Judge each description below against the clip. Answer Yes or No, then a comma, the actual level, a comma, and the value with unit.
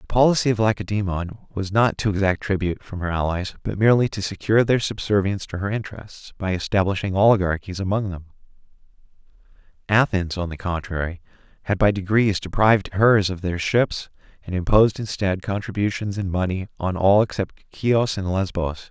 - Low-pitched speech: Yes, low, 100 Hz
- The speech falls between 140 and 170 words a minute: Yes, average, 160 wpm